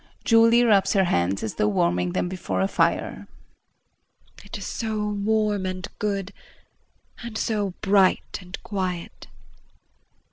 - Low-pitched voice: No, high, 195 Hz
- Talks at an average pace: No, slow, 130 wpm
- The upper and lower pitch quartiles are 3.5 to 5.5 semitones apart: No, average, 2.9 semitones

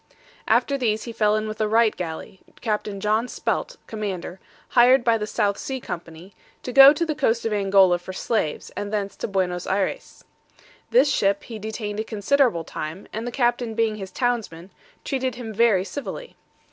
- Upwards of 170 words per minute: Yes, average, 180 wpm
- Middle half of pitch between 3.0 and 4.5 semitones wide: Yes, average, 3.7 semitones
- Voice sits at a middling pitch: No, high, 215 Hz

